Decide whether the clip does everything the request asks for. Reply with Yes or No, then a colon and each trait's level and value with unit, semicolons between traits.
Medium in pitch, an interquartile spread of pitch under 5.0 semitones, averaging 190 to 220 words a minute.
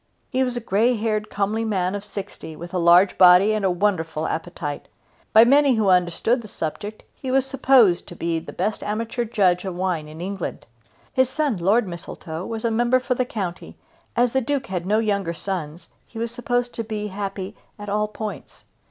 No: high, 205 Hz; average, 4.6 semitones; average, 195 wpm